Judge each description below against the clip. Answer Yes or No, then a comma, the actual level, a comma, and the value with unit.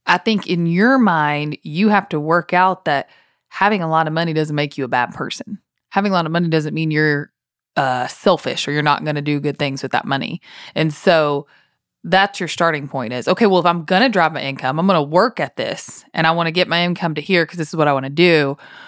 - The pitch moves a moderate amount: Yes, average, 3.7 semitones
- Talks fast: Yes, fast, 260 wpm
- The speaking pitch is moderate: Yes, medium, 165 Hz